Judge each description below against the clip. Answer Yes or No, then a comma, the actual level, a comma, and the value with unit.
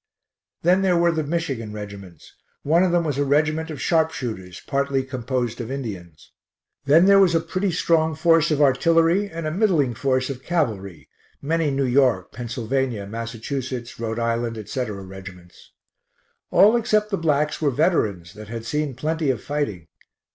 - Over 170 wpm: No, average, 160 wpm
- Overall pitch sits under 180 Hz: Yes, low, 135 Hz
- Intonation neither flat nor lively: No, wide, 6.1 semitones